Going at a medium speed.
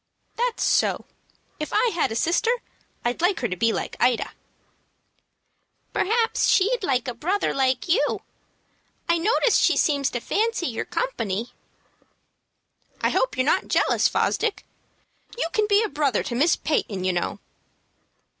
Yes: average, 145 wpm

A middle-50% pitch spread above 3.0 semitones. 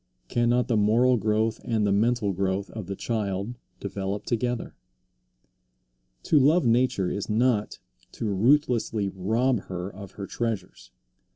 Yes: average, 3.4 semitones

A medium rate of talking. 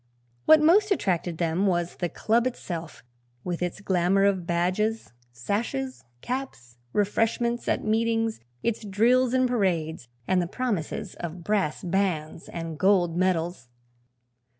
No: slow, 125 wpm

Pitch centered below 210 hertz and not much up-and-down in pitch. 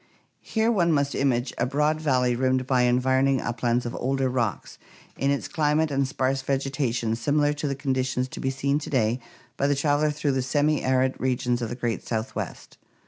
Yes: low, 135 Hz; narrow, 2.3 semitones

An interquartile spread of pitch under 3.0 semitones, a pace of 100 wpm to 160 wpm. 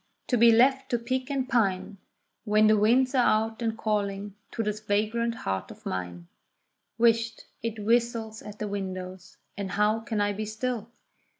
No: narrow, 2.4 semitones; average, 170 wpm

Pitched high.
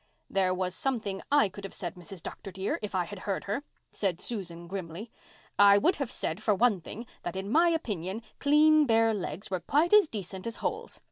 Yes: high, 200 Hz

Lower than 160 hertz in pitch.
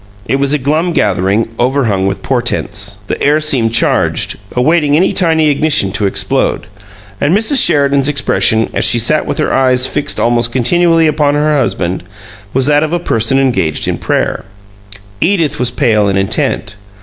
Yes: low, 135 Hz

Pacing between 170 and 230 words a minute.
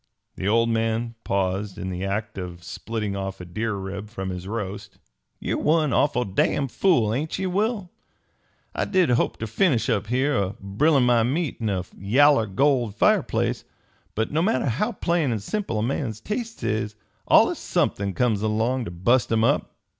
Yes: average, 175 wpm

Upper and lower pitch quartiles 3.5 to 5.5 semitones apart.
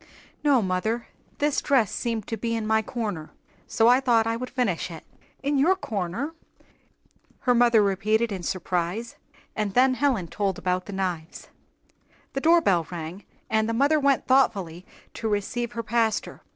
Yes: average, 4.7 semitones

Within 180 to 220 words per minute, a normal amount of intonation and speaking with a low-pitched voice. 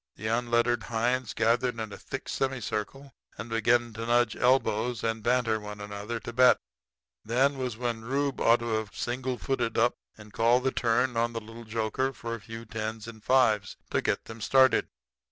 No: average, 185 wpm; narrow, 1.9 semitones; low, 115 Hz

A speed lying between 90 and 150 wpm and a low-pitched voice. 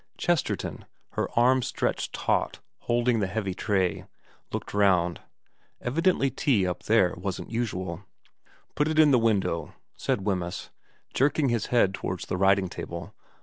Yes: average, 145 wpm; low, 105 Hz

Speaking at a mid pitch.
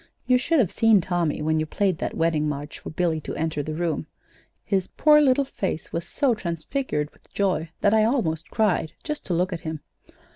Yes: medium, 175 Hz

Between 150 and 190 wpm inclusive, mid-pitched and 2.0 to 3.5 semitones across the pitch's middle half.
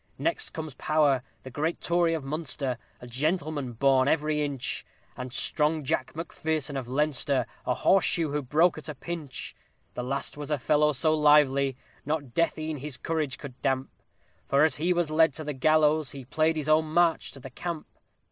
Yes: average, 185 wpm; medium, 150 Hz; average, 2.7 semitones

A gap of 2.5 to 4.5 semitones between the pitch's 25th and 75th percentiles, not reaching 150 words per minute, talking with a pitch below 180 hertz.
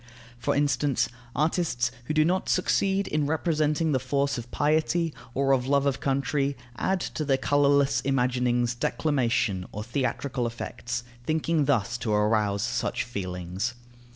Yes: average, 3.8 semitones; average, 140 wpm; low, 135 Hz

